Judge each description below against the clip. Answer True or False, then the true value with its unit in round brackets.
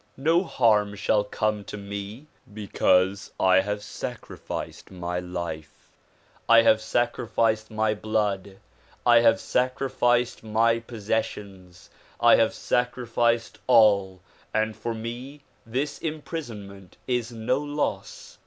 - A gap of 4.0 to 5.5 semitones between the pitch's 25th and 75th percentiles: False (3.2 semitones)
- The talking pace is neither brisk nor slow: False (115 wpm)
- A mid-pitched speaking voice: False (110 Hz)